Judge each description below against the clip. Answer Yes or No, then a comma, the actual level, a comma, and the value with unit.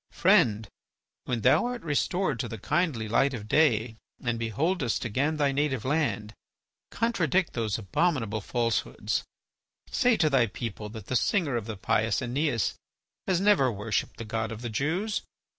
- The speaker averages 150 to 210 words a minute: Yes, average, 155 wpm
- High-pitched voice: No, low, 125 Hz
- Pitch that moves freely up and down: Yes, wide, 6.0 semitones